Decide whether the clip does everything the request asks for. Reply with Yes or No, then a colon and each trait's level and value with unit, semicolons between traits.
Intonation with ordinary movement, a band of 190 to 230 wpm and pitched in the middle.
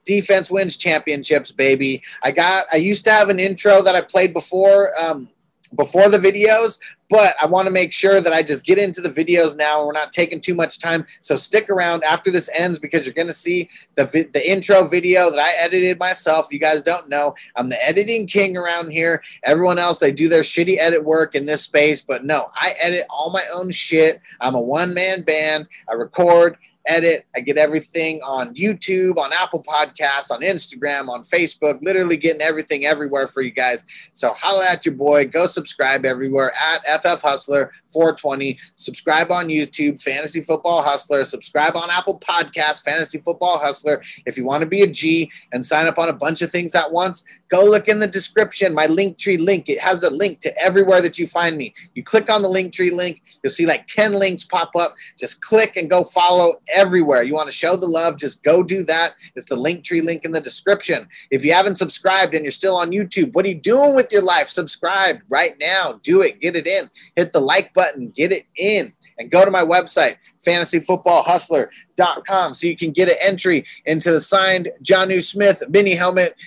Yes: average, 3.4 semitones; fast, 205 wpm; medium, 170 Hz